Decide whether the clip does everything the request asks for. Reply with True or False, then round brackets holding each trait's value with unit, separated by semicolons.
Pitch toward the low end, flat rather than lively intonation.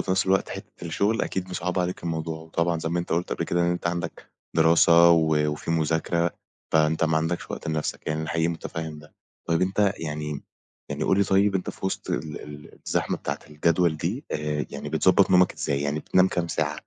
True (85 Hz; 2.3 semitones)